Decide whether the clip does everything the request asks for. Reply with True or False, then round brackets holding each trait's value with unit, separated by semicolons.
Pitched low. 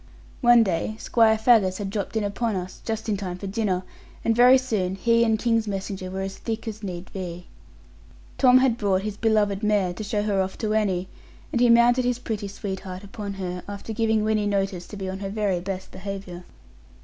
False (205 Hz)